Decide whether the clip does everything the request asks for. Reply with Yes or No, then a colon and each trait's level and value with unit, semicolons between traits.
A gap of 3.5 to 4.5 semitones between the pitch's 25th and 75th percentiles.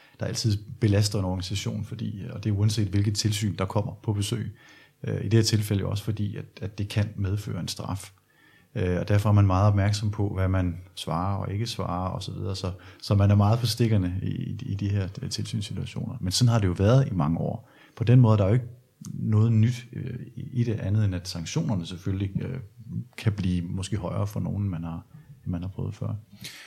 No: average, 3.1 semitones